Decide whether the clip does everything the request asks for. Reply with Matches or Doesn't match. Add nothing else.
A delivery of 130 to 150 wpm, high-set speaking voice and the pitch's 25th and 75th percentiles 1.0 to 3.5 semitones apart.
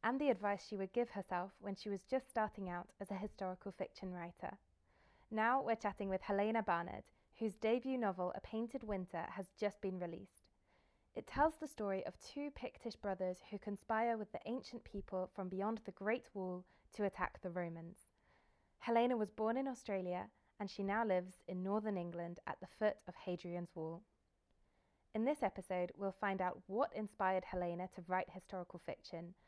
Doesn't match